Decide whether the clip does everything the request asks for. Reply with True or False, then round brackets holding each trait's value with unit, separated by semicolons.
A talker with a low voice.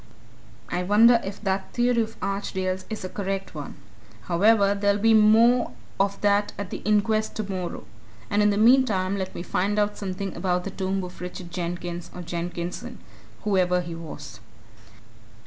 False (195 Hz)